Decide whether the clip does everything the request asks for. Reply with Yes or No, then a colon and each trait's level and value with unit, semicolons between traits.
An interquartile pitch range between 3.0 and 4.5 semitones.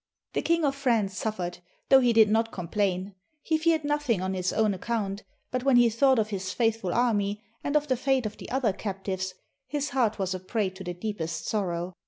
No: average, 5.0 semitones